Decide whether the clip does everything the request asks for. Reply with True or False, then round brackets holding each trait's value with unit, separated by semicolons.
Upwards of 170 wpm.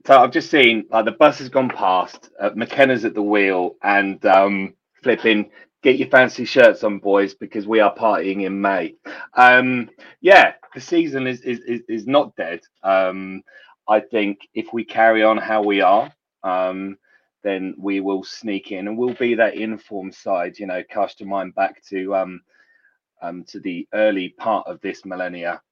True (180 wpm)